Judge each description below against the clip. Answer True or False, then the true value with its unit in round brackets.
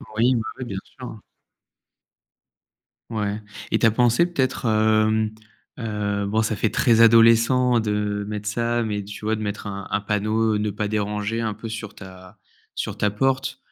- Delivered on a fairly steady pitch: True (1.8 semitones)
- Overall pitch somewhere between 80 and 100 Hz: False (110 Hz)